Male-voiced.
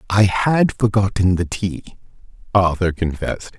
Yes: male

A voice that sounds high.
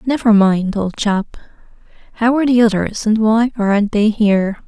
Yes: high, 215 Hz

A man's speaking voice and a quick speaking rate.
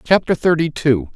No: male; average, 155 wpm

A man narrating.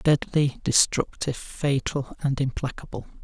Yes: male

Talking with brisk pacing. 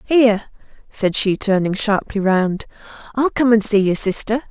No: average, 160 wpm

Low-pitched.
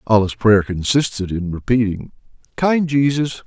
Yes: low, 115 Hz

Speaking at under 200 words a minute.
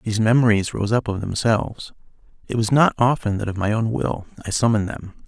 No: fast, 205 wpm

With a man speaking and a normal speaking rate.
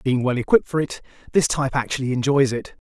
No: male; fast, 210 wpm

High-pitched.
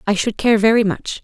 Yes: high, 215 Hz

